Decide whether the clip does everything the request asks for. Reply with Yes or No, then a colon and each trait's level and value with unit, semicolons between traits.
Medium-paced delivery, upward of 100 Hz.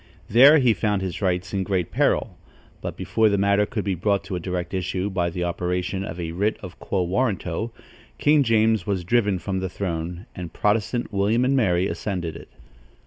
No: average, 195 wpm; very low, 95 Hz